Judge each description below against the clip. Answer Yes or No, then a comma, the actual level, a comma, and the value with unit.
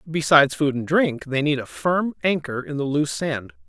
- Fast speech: Yes, fast, 210 wpm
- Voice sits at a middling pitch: Yes, medium, 145 Hz